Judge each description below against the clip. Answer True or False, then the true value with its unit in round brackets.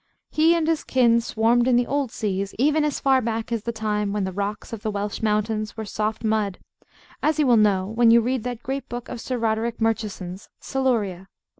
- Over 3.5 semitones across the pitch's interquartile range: False (2.9 semitones)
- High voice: True (225 Hz)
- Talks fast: True (210 wpm)